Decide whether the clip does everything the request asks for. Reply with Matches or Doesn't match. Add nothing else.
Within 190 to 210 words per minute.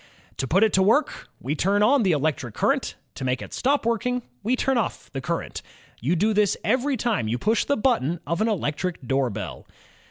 Matches